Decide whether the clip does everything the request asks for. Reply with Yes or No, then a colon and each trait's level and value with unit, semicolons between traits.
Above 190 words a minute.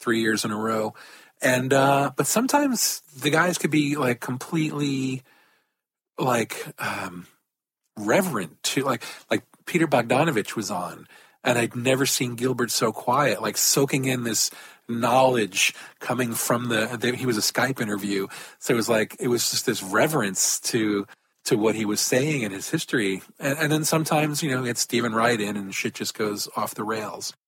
No: average, 175 wpm